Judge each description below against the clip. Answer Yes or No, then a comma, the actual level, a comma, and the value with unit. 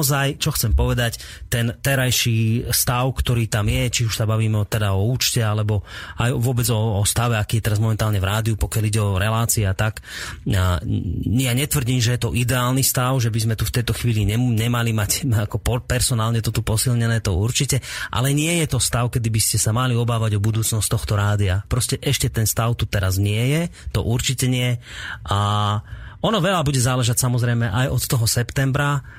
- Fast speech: Yes, fast, 190 wpm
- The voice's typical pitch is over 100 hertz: Yes, low, 115 Hz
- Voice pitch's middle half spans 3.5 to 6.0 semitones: No, narrow, 2.6 semitones